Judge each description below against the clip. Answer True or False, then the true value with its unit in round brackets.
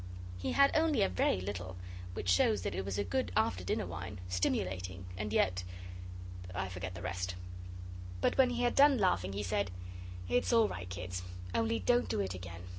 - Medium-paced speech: True (190 wpm)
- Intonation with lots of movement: False (3.5 semitones)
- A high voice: False (95 Hz)